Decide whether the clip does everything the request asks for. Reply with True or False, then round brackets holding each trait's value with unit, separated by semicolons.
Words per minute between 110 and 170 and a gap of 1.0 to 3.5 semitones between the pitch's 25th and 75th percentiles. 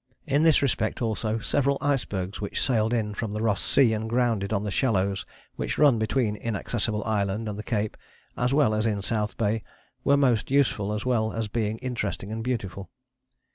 False (185 wpm; 2.8 semitones)